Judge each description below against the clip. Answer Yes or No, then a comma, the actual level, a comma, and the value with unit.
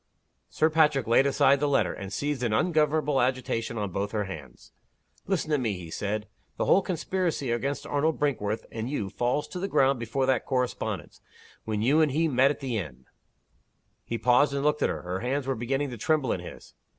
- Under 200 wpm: No, fast, 205 wpm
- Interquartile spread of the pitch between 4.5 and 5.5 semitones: Yes, average, 4.9 semitones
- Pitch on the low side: Yes, low, 130 Hz